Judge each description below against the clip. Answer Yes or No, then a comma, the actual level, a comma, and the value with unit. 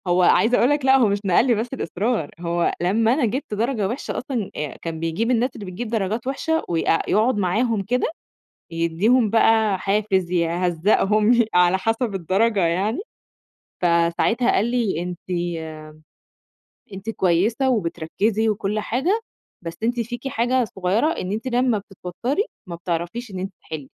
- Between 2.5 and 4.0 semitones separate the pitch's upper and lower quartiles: No, average, 5.0 semitones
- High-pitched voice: Yes, high, 210 Hz